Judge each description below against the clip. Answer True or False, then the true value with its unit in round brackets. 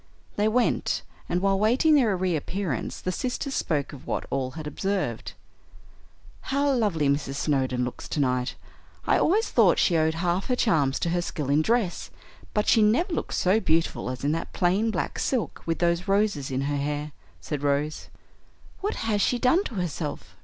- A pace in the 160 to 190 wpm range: True (175 wpm)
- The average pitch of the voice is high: False (175 Hz)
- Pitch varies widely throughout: True (6.9 semitones)